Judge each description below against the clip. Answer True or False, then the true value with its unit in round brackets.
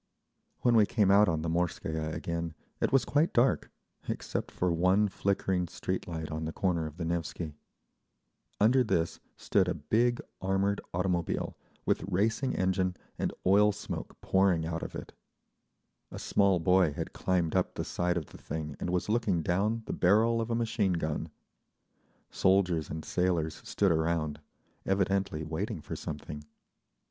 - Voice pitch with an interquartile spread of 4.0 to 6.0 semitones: False (3.6 semitones)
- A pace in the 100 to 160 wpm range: True (155 wpm)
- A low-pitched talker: True (90 Hz)